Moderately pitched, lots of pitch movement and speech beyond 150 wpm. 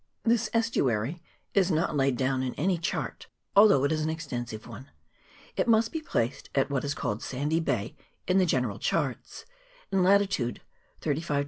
Yes: medium, 150 Hz; wide, 6.4 semitones; average, 180 wpm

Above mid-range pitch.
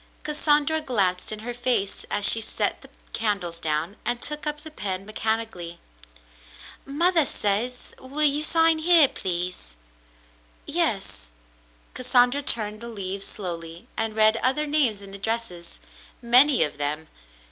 Yes: high, 225 Hz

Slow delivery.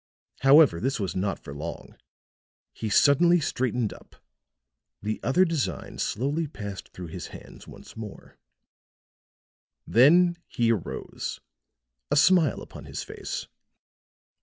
Yes: slow, 115 wpm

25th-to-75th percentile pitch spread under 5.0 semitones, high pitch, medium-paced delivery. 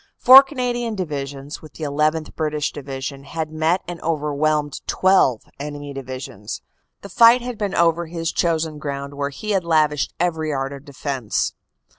No: average, 3.4 semitones; medium, 155 Hz; average, 160 wpm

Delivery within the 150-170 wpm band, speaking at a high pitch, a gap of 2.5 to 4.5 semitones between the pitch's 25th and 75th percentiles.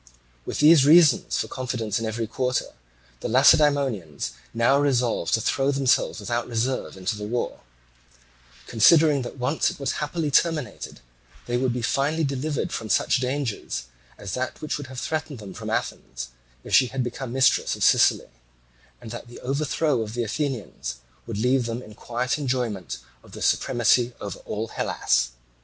No: average, 165 wpm; low, 125 Hz; average, 3.7 semitones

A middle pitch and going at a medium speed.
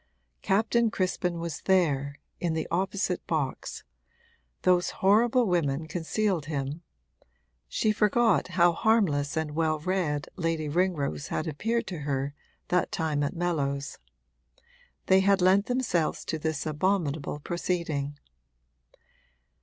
No: medium, 170 Hz; slow, 115 wpm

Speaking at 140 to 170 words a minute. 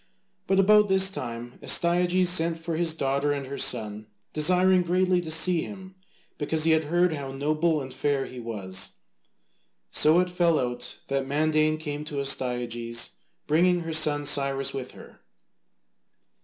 Yes: average, 155 wpm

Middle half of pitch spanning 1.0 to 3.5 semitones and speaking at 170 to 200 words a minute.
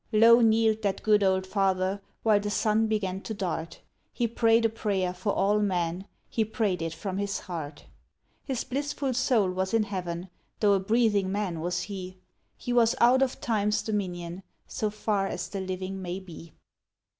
Yes: average, 3.0 semitones; average, 175 wpm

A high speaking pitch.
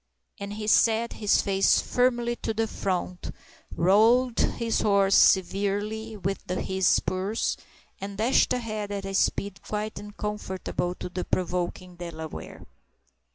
Yes: high, 200 Hz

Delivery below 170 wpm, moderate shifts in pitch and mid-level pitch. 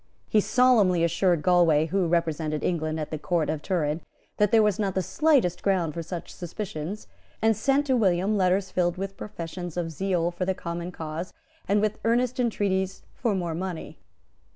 No: average, 175 wpm; average, 3.5 semitones; medium, 180 Hz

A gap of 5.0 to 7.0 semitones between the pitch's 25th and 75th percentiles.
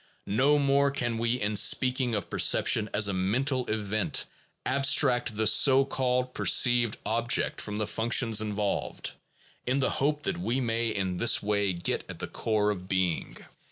No: average, 3.7 semitones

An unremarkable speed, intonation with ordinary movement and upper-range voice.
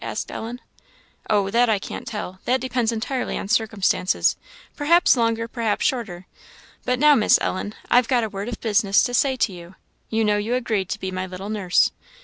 Yes: average, 190 wpm; average, 3.7 semitones; high, 220 Hz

